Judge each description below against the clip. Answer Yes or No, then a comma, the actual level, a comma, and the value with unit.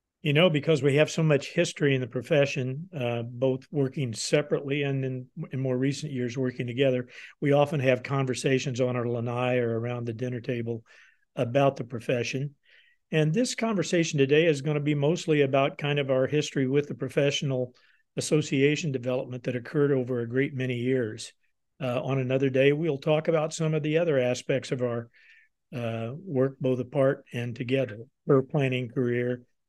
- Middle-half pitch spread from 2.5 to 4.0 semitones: Yes, average, 2.8 semitones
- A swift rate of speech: No, average, 175 wpm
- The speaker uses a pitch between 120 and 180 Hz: Yes, low, 135 Hz